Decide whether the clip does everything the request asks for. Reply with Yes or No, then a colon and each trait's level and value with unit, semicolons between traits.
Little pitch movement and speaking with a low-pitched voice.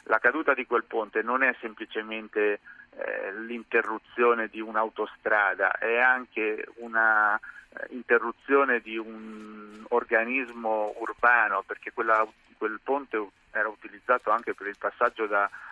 Yes: narrow, 1.7 semitones; low, 110 Hz